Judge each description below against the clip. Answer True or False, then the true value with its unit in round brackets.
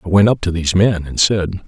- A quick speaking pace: True (285 wpm)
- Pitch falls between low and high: False (90 Hz)